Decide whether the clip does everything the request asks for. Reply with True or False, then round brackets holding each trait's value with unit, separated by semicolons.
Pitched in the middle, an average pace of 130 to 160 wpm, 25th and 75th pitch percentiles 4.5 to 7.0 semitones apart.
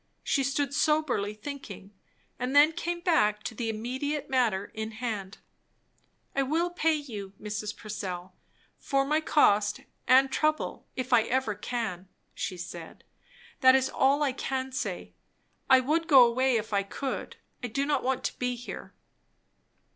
False (255 Hz; 155 wpm; 5.0 semitones)